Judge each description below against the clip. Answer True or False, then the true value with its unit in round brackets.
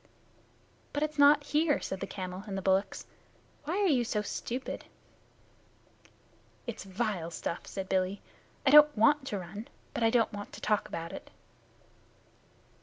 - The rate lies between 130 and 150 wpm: False (160 wpm)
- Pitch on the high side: True (215 Hz)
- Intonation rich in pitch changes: True (7.0 semitones)